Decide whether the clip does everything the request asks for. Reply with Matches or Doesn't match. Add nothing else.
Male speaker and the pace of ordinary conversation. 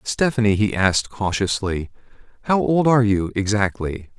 Doesn't match